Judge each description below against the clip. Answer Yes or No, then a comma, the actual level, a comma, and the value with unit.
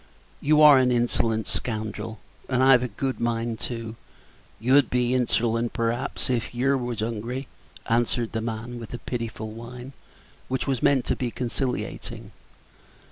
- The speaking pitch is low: Yes, low, 120 Hz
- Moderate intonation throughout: No, narrow, 1.9 semitones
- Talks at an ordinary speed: Yes, average, 150 wpm